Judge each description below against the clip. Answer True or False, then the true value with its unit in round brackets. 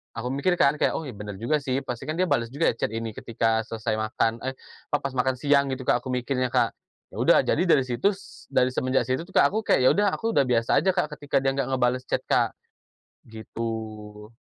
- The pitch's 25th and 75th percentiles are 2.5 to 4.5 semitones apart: True (3.8 semitones)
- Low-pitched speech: True (130 Hz)